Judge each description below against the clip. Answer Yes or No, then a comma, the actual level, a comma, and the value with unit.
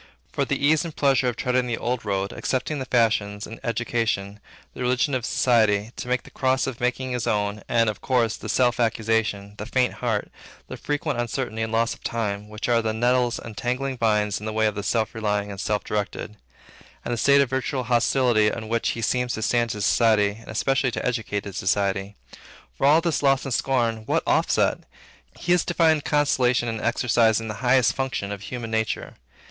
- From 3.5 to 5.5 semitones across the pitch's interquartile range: No, average, 3.0 semitones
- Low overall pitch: Yes, low, 115 Hz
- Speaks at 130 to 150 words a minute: No, fast, 205 wpm